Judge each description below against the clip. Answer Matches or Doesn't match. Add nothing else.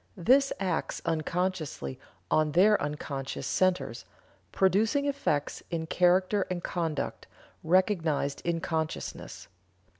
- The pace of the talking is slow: Matches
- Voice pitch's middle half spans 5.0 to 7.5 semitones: Doesn't match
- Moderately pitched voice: Matches